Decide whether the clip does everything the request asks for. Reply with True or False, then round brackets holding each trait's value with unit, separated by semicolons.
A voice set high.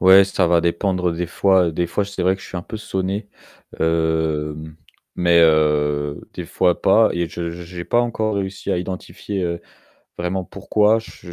False (90 Hz)